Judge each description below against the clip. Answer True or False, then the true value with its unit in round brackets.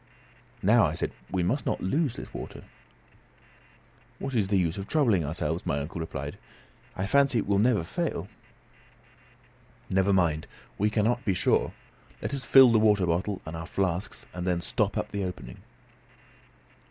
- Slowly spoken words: False (165 wpm)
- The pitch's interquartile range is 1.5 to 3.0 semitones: False (4.3 semitones)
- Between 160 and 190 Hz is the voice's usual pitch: False (95 Hz)